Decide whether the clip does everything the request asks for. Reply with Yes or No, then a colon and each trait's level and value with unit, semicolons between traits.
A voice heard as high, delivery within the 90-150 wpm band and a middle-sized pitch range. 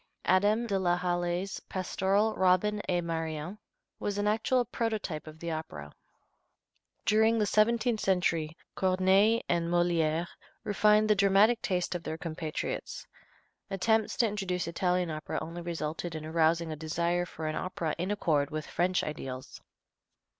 No: medium, 180 Hz; average, 140 wpm; average, 4.1 semitones